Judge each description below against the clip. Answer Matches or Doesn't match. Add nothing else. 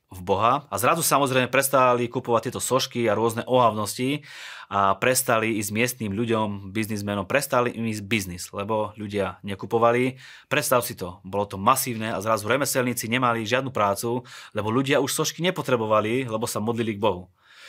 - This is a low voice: Matches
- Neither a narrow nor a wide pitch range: Matches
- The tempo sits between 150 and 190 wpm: Matches